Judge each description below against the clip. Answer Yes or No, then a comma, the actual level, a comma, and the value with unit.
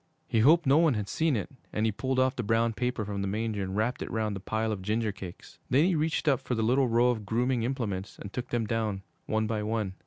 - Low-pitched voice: Yes, low, 115 Hz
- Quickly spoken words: Yes, fast, 260 wpm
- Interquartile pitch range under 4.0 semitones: Yes, average, 3.1 semitones